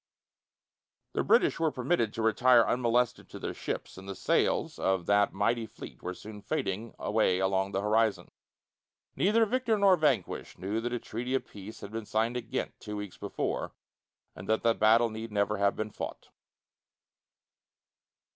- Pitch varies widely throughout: No, average, 3.2 semitones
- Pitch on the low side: Yes, low, 110 Hz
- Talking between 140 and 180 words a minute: Yes, average, 165 wpm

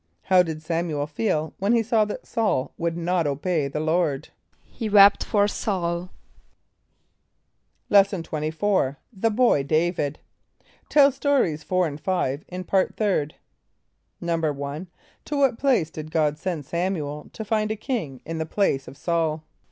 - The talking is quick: No, average, 155 wpm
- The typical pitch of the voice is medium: Yes, medium, 170 Hz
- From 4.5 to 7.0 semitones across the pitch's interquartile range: Yes, average, 4.9 semitones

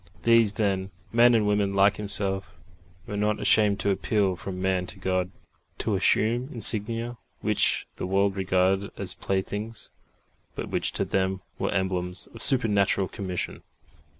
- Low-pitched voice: Yes, low, 100 Hz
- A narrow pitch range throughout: Yes, narrow, 2.1 semitones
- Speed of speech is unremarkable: Yes, average, 145 wpm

